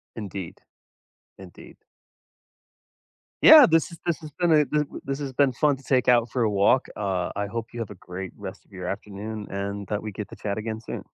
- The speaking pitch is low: Yes, low, 110 Hz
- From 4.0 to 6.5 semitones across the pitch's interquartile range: Yes, wide, 5.4 semitones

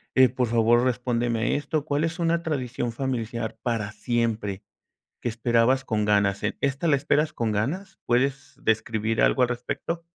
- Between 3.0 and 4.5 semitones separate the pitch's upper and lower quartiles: Yes, average, 3.6 semitones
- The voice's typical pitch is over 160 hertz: No, low, 120 Hz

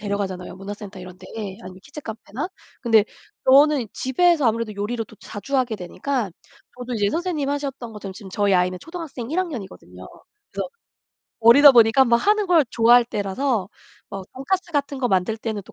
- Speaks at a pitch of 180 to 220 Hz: No, high, 230 Hz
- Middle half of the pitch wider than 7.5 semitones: No, wide, 5.6 semitones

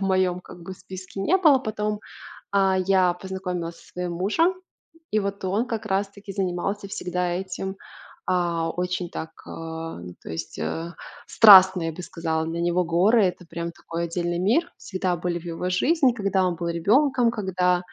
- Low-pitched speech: No, medium, 185 Hz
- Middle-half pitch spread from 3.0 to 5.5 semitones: No, narrow, 2.5 semitones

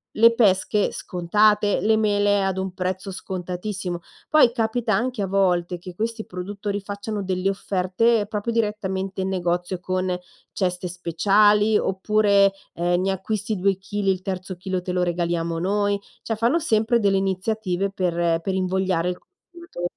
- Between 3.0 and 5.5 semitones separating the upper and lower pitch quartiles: No, narrow, 2.5 semitones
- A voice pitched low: No, high, 195 Hz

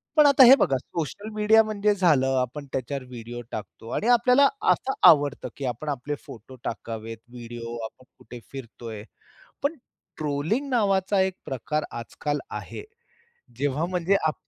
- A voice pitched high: No, medium, 145 Hz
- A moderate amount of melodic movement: No, wide, 8.9 semitones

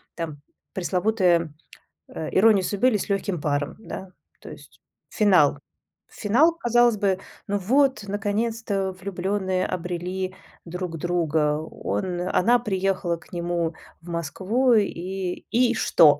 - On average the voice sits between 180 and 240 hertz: Yes, high, 190 Hz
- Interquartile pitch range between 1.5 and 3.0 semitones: No, average, 3.4 semitones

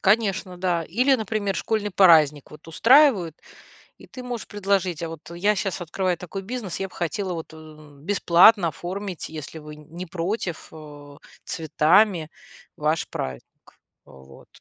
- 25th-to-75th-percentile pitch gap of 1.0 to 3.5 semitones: No, average, 4.3 semitones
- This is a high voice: No, medium, 180 Hz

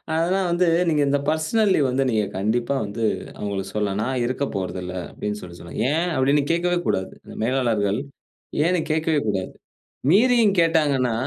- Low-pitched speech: Yes, low, 130 Hz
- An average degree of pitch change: No, wide, 7.8 semitones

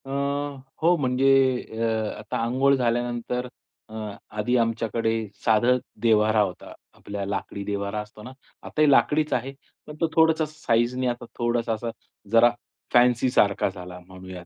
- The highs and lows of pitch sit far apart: No, average, 3.7 semitones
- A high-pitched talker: No, low, 120 Hz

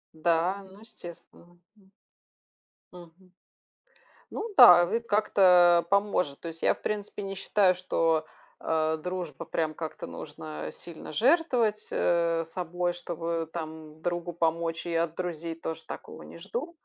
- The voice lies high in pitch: No, medium, 175 Hz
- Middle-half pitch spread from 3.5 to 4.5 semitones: No, average, 2.8 semitones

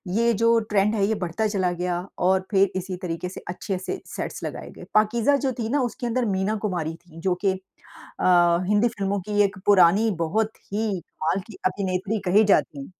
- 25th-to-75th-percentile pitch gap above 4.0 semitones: No, average, 3.3 semitones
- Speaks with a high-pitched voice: Yes, high, 195 Hz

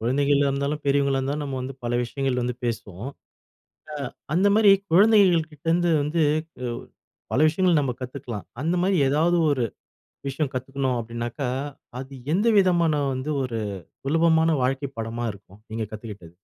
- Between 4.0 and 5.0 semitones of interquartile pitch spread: Yes, average, 4.7 semitones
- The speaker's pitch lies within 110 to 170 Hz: Yes, medium, 140 Hz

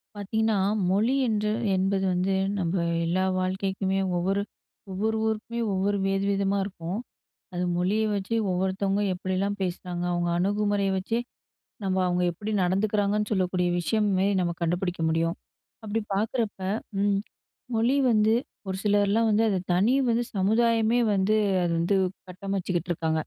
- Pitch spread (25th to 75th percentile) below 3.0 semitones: Yes, narrow, 2.4 semitones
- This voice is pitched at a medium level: No, high, 195 Hz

